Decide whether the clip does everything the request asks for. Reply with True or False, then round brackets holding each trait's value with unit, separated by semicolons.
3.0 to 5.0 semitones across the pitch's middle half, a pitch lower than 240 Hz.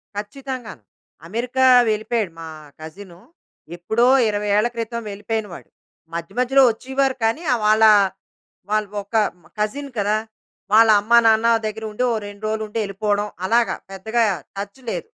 False (2.4 semitones; 215 Hz)